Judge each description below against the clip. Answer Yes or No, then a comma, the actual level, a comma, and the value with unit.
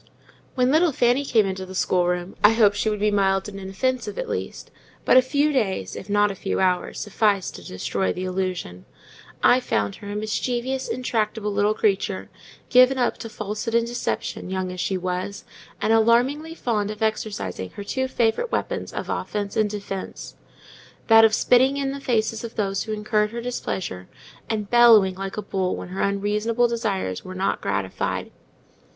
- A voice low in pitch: No, high, 210 Hz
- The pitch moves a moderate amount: Yes, average, 3.8 semitones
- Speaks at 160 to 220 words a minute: Yes, average, 180 wpm